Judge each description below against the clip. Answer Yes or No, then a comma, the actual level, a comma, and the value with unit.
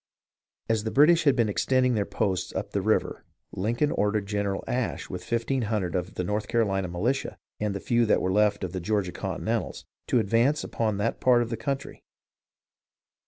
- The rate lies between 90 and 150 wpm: No, average, 185 wpm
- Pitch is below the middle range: Yes, low, 110 Hz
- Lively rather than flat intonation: No, average, 3.3 semitones